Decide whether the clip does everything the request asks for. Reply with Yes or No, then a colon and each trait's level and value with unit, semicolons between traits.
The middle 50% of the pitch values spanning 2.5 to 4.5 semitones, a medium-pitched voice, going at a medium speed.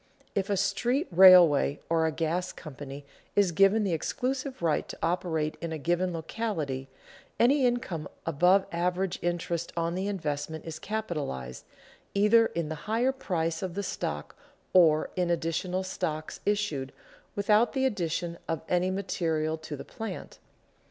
Yes: average, 4.1 semitones; medium, 175 Hz; average, 145 wpm